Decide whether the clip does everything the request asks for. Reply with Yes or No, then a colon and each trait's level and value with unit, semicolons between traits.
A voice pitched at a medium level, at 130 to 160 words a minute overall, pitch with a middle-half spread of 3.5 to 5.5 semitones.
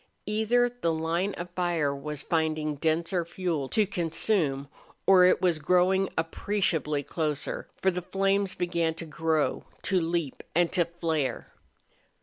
No: medium, 170 Hz; slow, 135 wpm; average, 2.8 semitones